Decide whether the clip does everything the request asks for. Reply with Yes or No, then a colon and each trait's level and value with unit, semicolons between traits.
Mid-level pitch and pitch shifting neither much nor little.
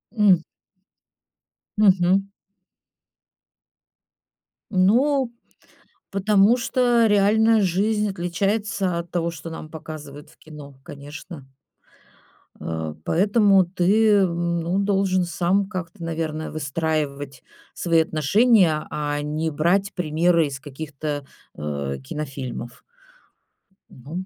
Yes: medium, 170 Hz; average, 4.6 semitones